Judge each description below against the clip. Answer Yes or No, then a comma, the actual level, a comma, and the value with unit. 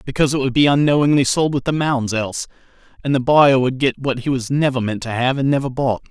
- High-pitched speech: No, low, 135 Hz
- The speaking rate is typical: No, fast, 245 wpm